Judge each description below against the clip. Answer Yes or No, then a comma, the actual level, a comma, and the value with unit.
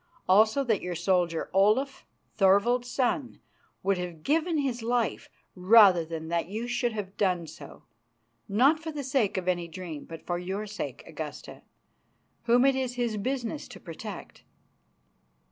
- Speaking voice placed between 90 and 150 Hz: No, high, 210 Hz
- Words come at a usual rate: Yes, average, 150 wpm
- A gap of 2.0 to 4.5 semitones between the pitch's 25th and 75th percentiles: No, wide, 5.5 semitones